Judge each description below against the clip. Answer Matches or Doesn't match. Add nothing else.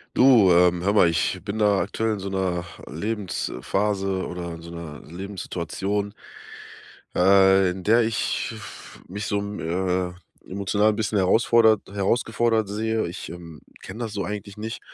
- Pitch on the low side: Matches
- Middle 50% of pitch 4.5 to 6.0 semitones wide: Doesn't match